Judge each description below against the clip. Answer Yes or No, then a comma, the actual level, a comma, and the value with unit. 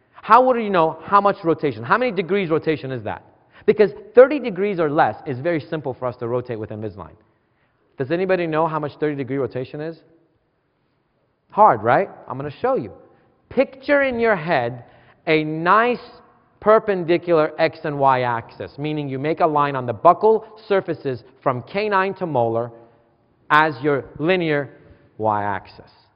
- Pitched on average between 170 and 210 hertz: No, medium, 155 Hz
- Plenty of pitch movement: Yes, wide, 7.3 semitones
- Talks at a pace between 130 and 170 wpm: Yes, average, 165 wpm